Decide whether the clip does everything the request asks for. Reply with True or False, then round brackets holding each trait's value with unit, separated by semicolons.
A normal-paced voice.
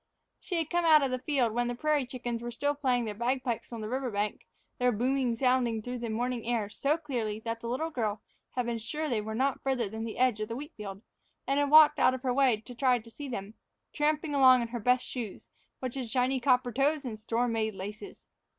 False (240 wpm)